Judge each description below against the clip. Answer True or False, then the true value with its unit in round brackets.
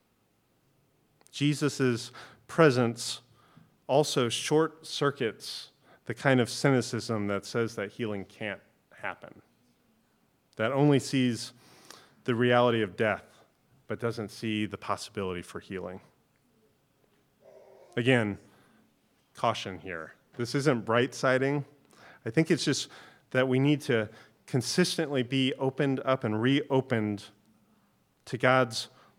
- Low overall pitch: True (125 Hz)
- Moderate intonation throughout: True (3.6 semitones)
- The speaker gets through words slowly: True (105 wpm)